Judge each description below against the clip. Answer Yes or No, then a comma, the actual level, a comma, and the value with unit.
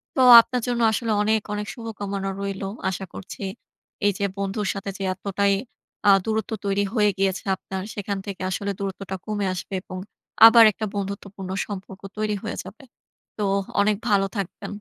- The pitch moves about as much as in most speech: No, narrow, 1.5 semitones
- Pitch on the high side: Yes, high, 200 Hz